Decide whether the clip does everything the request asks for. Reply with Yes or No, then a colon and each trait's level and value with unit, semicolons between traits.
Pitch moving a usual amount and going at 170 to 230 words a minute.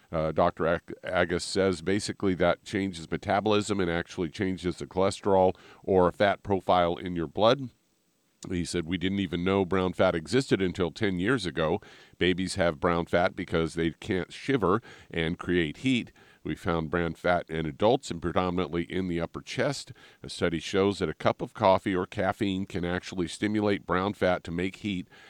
No: narrow, 2.2 semitones; average, 175 wpm